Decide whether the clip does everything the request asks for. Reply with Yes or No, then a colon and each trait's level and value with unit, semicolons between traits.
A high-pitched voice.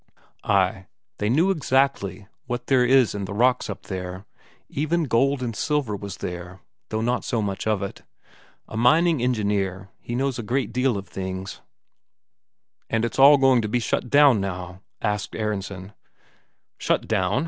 No: low, 110 Hz